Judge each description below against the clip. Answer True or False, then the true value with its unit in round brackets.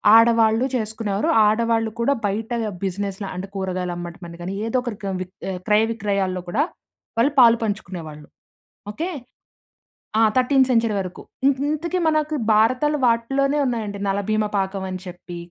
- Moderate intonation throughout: True (3.7 semitones)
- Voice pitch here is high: True (215 Hz)